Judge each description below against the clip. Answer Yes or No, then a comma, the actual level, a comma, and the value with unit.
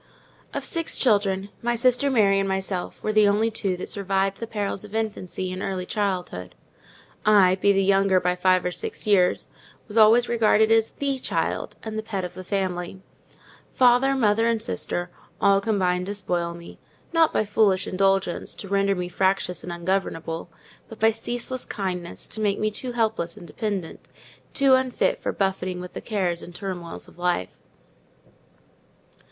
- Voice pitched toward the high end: Yes, high, 195 Hz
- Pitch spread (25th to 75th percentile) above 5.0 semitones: No, average, 3.2 semitones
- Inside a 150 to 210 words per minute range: Yes, average, 165 wpm